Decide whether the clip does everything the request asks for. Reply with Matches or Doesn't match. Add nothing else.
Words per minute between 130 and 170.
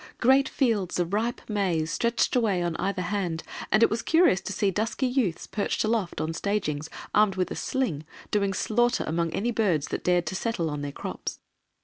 Doesn't match